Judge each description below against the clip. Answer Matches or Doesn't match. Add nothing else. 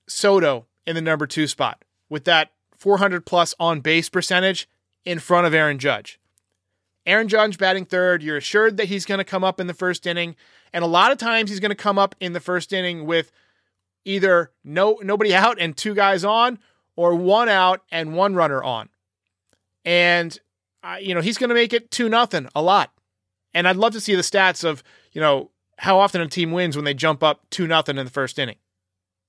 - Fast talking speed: Matches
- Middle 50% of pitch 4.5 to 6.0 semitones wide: Matches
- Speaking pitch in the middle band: Matches